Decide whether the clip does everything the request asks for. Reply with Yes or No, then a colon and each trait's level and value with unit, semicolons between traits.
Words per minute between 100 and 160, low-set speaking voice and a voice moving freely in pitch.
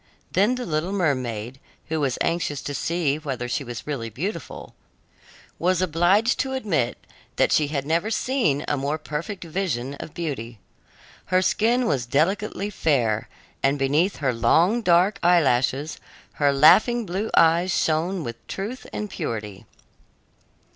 No: average, 140 wpm; medium, 160 Hz; wide, 5.9 semitones